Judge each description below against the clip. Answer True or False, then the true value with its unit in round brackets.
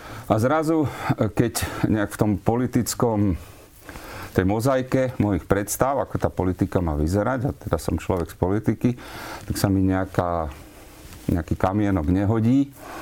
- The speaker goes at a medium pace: True (135 wpm)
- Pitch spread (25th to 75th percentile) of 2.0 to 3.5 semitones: False (4.3 semitones)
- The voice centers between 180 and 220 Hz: False (105 Hz)